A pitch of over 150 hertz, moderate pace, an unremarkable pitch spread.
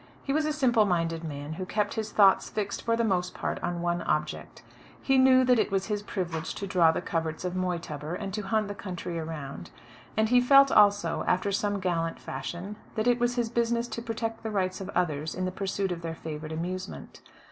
No: high, 190 Hz; fast, 215 wpm; average, 4.7 semitones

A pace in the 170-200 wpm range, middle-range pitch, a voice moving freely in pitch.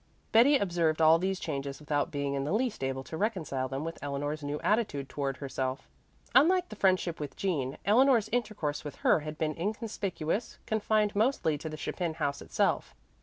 Yes: average, 175 wpm; medium, 160 Hz; wide, 6.6 semitones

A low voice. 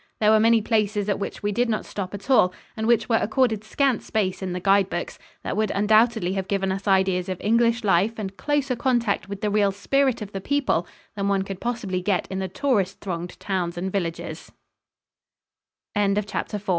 No: high, 205 Hz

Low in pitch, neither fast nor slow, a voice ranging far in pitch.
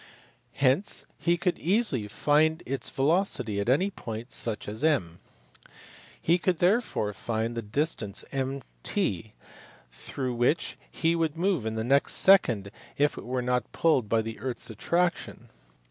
Yes: low, 130 Hz; average, 145 wpm; wide, 6.7 semitones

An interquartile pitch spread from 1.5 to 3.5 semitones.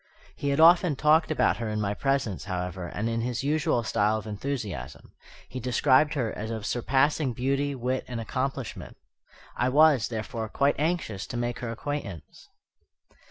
No: average, 4.5 semitones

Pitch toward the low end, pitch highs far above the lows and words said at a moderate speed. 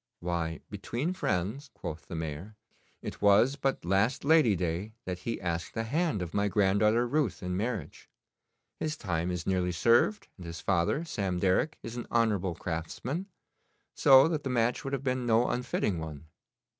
Yes: low, 105 Hz; wide, 6.1 semitones; average, 170 wpm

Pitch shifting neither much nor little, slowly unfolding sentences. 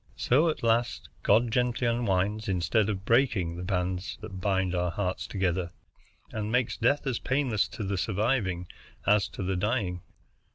No: average, 4.0 semitones; average, 160 wpm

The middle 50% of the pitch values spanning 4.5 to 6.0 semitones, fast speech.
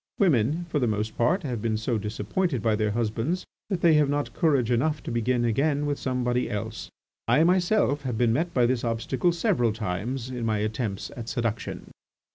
No: average, 4.9 semitones; average, 190 wpm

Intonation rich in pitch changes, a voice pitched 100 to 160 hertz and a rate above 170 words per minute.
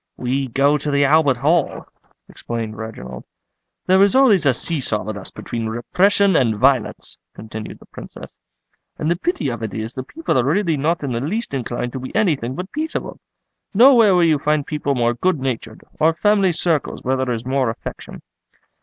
Yes: wide, 6.4 semitones; medium, 140 Hz; average, 190 wpm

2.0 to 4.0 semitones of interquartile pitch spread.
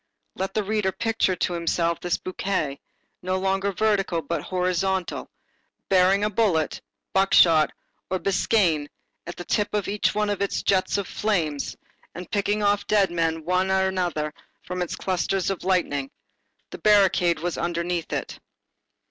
Yes: narrow, 2.6 semitones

